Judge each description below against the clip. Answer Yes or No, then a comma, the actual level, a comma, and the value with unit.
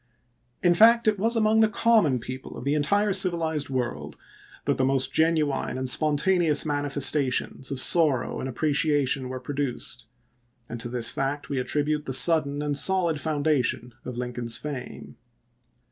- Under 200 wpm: Yes, average, 155 wpm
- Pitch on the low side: No, medium, 145 Hz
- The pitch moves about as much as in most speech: Yes, average, 4.0 semitones